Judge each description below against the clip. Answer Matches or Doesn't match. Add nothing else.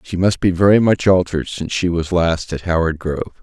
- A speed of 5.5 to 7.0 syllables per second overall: Matches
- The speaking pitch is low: Matches